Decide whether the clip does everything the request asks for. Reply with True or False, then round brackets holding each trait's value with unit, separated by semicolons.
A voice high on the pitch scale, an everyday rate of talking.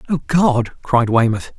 False (130 Hz; 150 wpm)